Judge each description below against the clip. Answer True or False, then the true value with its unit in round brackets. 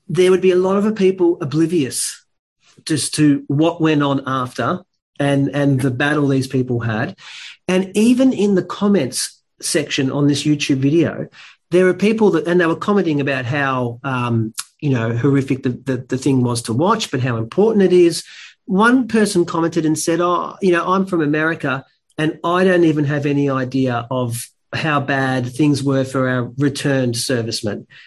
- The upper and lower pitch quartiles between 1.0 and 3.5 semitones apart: False (4.9 semitones)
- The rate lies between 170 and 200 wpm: True (180 wpm)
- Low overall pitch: False (145 Hz)